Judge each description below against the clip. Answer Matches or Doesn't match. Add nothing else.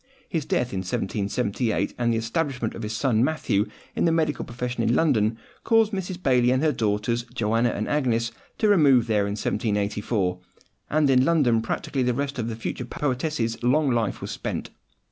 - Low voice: Matches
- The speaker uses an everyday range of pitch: Matches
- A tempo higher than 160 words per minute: Matches